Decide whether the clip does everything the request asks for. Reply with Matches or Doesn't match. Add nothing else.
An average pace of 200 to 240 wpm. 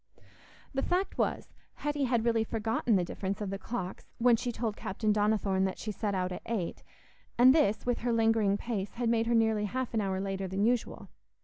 Matches